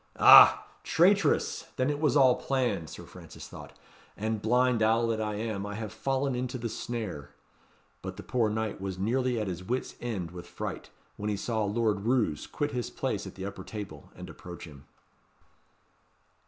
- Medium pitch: No, low, 110 Hz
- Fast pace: No, average, 180 wpm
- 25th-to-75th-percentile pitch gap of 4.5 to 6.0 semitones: No, average, 4.0 semitones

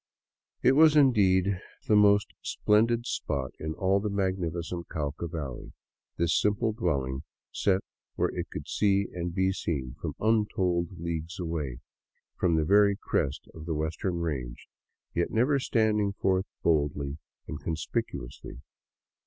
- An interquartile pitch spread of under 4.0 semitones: No, average, 4.6 semitones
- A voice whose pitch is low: Yes, very low, 90 Hz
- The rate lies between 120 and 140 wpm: Yes, slow, 135 wpm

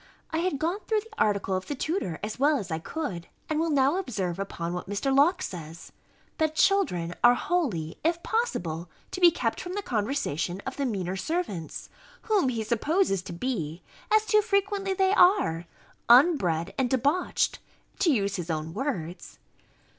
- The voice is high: Yes, very high, 260 Hz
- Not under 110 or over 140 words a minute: No, average, 170 wpm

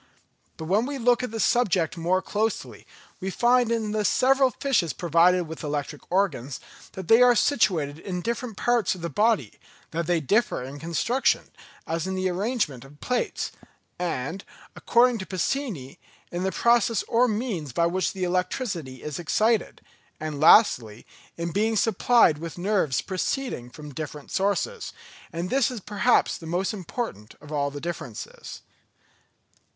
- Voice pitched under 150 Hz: No, medium, 185 Hz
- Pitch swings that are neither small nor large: No, wide, 6.3 semitones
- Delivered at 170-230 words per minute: No, average, 155 wpm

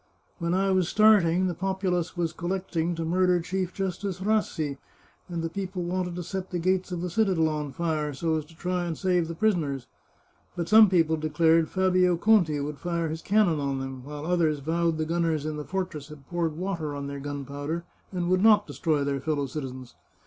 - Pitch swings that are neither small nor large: Yes, average, 3.2 semitones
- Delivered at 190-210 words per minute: Yes, average, 200 wpm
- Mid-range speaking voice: Yes, medium, 170 Hz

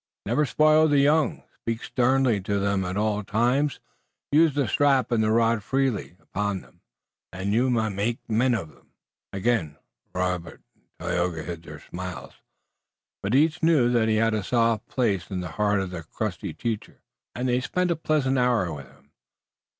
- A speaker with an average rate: Yes, average, 175 wpm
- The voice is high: No, low, 115 Hz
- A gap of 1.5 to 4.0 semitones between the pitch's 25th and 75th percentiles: No, average, 5.2 semitones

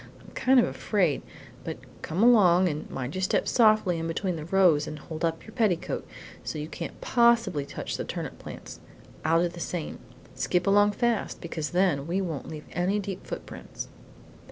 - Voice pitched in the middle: Yes, medium, 180 Hz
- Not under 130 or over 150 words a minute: No, average, 180 wpm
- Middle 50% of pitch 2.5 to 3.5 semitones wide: No, average, 4.2 semitones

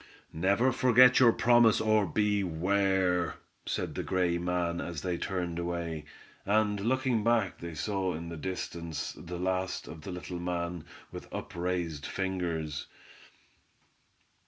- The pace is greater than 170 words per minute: No, slow, 135 wpm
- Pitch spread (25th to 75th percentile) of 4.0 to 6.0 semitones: No, average, 3.2 semitones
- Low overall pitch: Yes, very low, 90 Hz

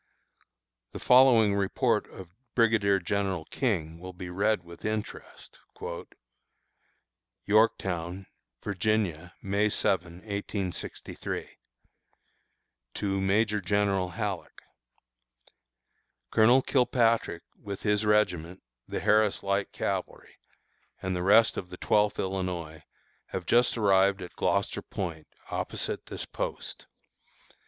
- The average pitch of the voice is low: Yes, low, 100 Hz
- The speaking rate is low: Yes, slow, 100 wpm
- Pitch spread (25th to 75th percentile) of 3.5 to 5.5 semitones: No, average, 2.9 semitones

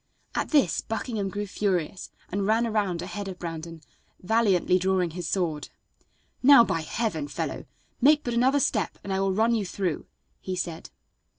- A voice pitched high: Yes, high, 195 Hz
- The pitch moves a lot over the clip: No, average, 4.2 semitones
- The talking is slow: No, average, 165 wpm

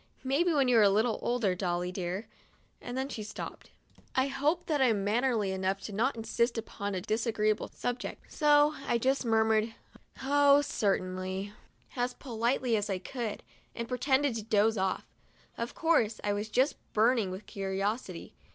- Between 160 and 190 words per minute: Yes, average, 170 wpm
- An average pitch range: Yes, average, 4.3 semitones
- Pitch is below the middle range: No, high, 225 Hz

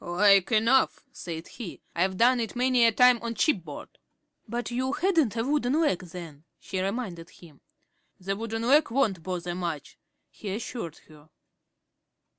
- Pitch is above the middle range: Yes, high, 215 Hz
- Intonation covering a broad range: Yes, wide, 5.9 semitones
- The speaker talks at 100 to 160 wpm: Yes, average, 150 wpm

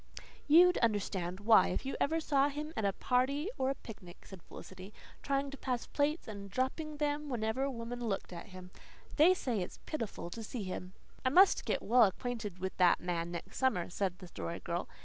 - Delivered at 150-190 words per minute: No, average, 200 wpm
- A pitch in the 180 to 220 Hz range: No, high, 230 Hz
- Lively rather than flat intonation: Yes, wide, 6.7 semitones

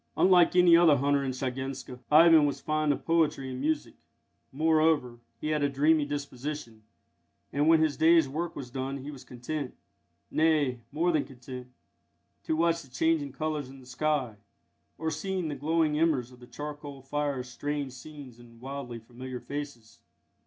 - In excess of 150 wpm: Yes, average, 165 wpm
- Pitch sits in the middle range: Yes, medium, 145 Hz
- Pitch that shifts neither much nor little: Yes, average, 3.3 semitones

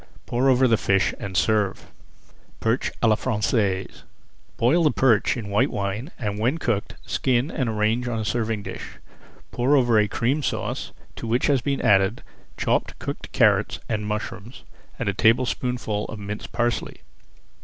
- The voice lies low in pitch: Yes, low, 115 Hz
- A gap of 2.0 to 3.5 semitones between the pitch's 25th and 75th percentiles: Yes, average, 3.1 semitones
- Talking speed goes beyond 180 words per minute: No, average, 160 wpm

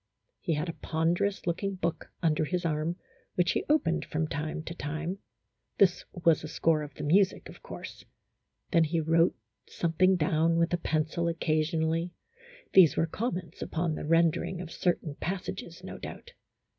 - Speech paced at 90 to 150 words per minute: No, average, 165 wpm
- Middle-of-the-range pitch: Yes, medium, 165 Hz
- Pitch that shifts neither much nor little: No, narrow, 1.9 semitones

